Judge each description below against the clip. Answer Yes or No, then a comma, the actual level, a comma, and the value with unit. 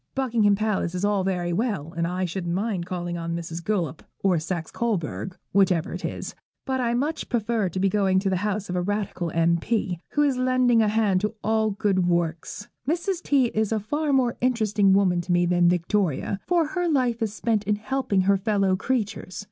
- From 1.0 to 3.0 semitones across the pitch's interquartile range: No, average, 4.5 semitones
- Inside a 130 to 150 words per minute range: No, average, 200 wpm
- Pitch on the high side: Yes, high, 200 Hz